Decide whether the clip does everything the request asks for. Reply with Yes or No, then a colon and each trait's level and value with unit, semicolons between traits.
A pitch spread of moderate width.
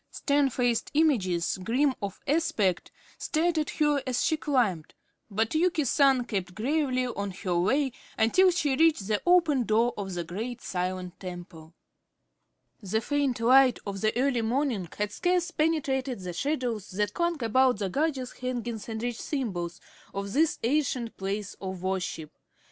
No: wide, 6.5 semitones